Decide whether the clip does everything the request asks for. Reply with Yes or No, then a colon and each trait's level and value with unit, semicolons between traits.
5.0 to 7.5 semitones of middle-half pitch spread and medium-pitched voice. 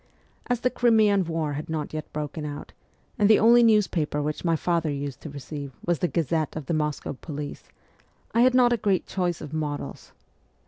Yes: wide, 5.5 semitones; medium, 160 Hz